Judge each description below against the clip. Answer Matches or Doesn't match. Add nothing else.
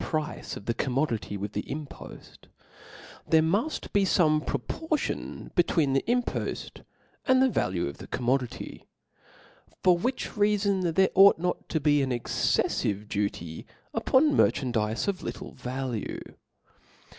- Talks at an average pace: Doesn't match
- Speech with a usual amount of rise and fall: Doesn't match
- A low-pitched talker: Doesn't match